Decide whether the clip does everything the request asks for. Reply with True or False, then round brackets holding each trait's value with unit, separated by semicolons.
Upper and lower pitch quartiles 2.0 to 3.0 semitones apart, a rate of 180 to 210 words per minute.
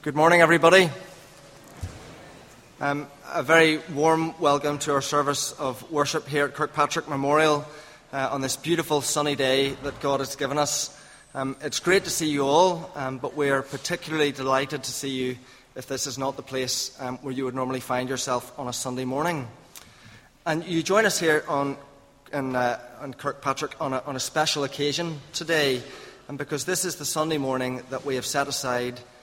True (2.4 semitones; 185 wpm)